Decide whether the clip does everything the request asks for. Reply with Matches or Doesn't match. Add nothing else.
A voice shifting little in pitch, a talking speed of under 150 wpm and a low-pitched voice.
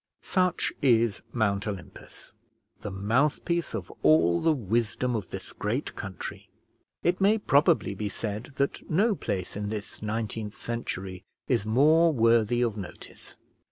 Doesn't match